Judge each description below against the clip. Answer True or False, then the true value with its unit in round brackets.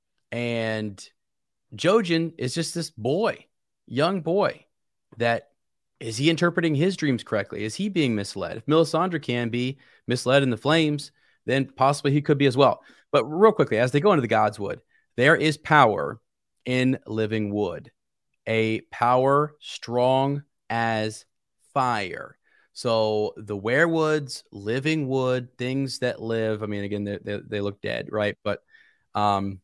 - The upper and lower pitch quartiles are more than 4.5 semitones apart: True (5.3 semitones)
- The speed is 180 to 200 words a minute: False (150 wpm)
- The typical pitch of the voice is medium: False (125 Hz)